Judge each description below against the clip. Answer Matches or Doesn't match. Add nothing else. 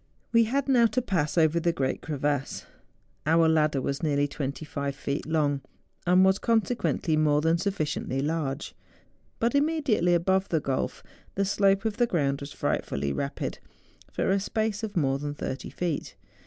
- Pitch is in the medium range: Matches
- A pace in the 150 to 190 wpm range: Matches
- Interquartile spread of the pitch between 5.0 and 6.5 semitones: Matches